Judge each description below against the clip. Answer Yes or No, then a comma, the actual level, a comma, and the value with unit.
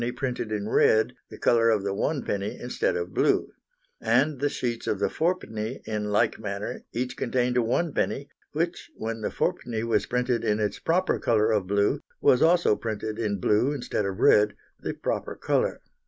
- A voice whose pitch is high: No, low, 115 Hz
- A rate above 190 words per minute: No, average, 175 wpm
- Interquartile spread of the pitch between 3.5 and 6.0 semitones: No, average, 3.1 semitones